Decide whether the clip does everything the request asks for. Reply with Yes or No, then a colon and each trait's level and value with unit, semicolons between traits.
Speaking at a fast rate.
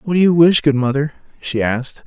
Yes: fast, 235 wpm